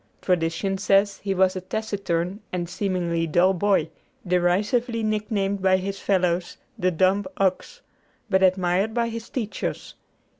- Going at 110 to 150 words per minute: Yes, slow, 135 wpm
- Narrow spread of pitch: Yes, narrow, 2.3 semitones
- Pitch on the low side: No, high, 190 Hz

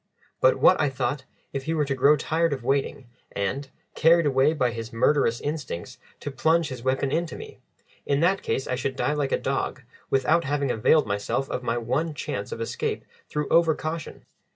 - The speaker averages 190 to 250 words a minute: Yes, average, 195 wpm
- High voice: No, medium, 140 Hz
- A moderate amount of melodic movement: Yes, average, 3.5 semitones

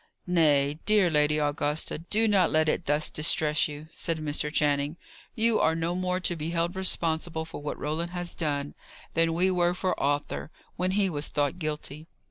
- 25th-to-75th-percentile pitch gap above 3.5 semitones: No, average, 2.9 semitones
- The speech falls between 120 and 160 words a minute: No, average, 180 wpm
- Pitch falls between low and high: Yes, medium, 160 Hz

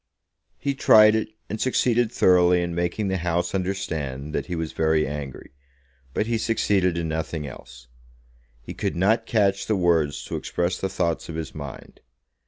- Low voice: Yes, very low, 90 Hz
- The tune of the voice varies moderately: Yes, average, 4.0 semitones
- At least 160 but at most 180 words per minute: Yes, average, 170 wpm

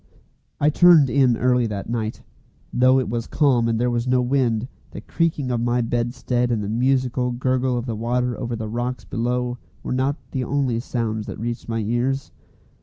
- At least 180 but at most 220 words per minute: Yes, average, 185 wpm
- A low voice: Yes, low, 125 Hz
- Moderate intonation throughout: No, narrow, 1.7 semitones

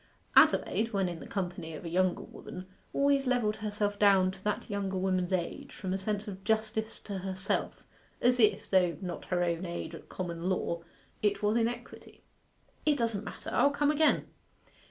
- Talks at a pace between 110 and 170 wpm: No, average, 180 wpm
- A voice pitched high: Yes, high, 200 Hz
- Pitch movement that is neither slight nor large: Yes, average, 3.0 semitones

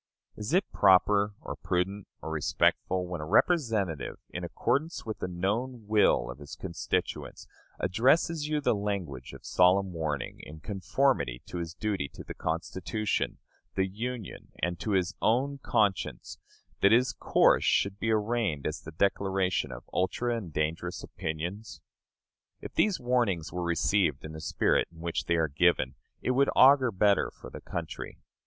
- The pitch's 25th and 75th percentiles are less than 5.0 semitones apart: No, average, 5.3 semitones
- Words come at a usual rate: Yes, average, 160 wpm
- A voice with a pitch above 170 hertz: No, very low, 95 Hz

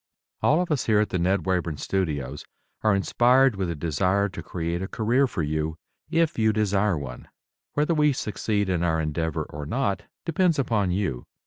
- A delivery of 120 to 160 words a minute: No, average, 185 wpm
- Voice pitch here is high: No, very low, 95 Hz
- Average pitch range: No, wide, 6.6 semitones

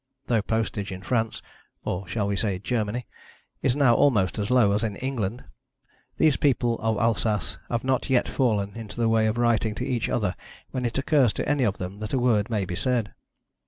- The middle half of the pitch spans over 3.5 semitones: No, average, 3.2 semitones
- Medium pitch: No, low, 115 Hz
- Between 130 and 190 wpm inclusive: No, average, 200 wpm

